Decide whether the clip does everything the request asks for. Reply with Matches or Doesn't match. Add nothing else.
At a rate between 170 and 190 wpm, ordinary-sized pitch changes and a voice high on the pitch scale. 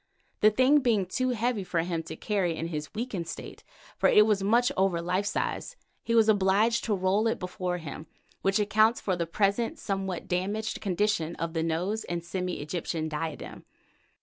Matches